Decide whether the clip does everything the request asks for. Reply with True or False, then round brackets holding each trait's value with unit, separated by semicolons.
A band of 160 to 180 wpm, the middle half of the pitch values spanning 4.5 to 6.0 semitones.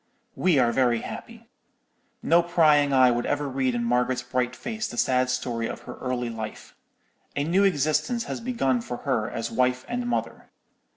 True (175 wpm; 5.2 semitones)